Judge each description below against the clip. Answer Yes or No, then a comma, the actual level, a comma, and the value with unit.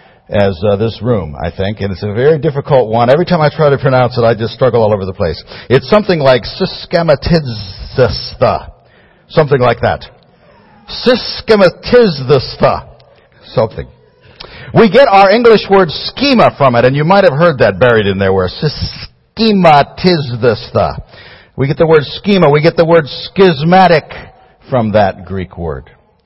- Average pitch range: No, wide, 8.5 semitones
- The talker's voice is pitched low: No, medium, 145 Hz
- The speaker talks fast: No, average, 155 wpm